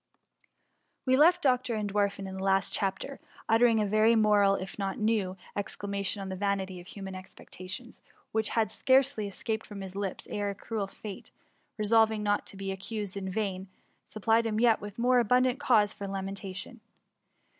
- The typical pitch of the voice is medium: No, high, 205 Hz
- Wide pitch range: No, narrow, 2.5 semitones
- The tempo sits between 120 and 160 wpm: No, average, 175 wpm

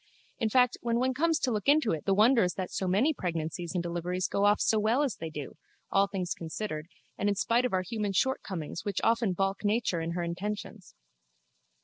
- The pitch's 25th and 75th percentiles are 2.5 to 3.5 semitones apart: No, average, 4.7 semitones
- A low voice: No, high, 200 Hz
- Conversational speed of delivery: No, fast, 215 wpm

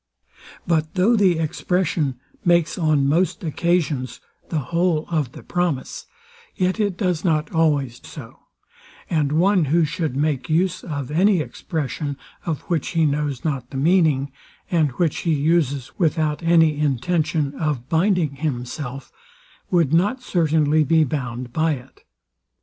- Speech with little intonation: No, average, 3.3 semitones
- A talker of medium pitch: Yes, medium, 155 Hz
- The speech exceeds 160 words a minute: No, average, 140 wpm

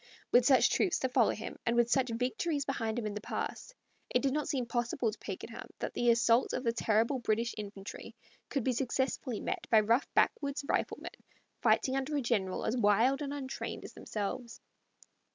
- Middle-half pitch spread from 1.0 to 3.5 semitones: Yes, average, 3.1 semitones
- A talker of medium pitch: No, high, 240 Hz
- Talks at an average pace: Yes, average, 190 wpm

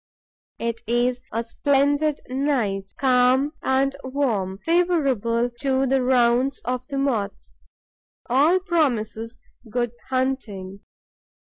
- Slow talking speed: Yes, slow, 100 wpm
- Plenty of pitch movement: No, average, 3.1 semitones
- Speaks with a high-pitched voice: Yes, very high, 255 Hz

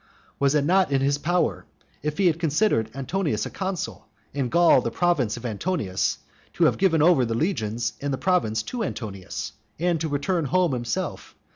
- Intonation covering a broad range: Yes, wide, 6.6 semitones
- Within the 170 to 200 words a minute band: Yes, average, 180 wpm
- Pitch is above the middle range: No, medium, 145 Hz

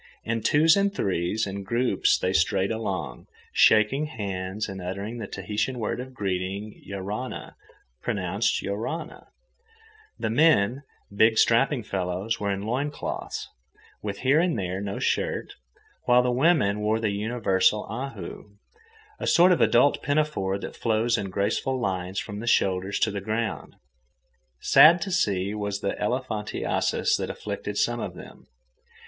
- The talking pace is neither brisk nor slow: Yes, average, 145 wpm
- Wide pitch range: No, average, 4.0 semitones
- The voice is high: No, low, 105 Hz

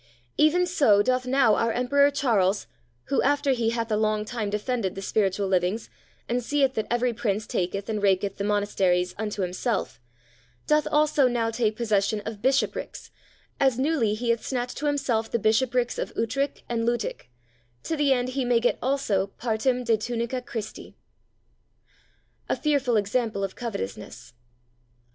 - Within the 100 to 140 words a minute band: No, average, 160 wpm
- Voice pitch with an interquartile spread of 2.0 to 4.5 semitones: Yes, average, 3.6 semitones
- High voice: Yes, high, 230 Hz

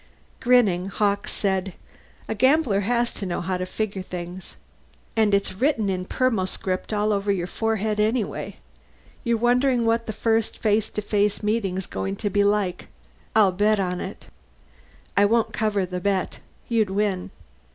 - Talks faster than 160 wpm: No, average, 155 wpm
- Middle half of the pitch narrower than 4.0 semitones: Yes, average, 2.9 semitones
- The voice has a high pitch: Yes, high, 205 Hz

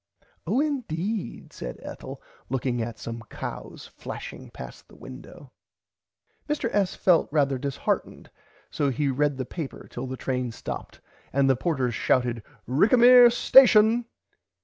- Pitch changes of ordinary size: No, wide, 9.0 semitones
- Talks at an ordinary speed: No, slow, 130 wpm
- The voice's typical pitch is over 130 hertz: Yes, medium, 140 Hz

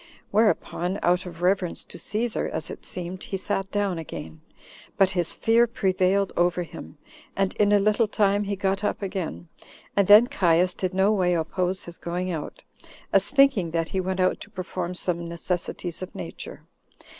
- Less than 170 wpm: No, average, 175 wpm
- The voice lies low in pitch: No, medium, 185 Hz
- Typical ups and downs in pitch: No, narrow, 2.3 semitones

